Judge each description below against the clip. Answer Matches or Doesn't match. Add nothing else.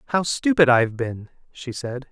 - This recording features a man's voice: Matches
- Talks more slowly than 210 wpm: Matches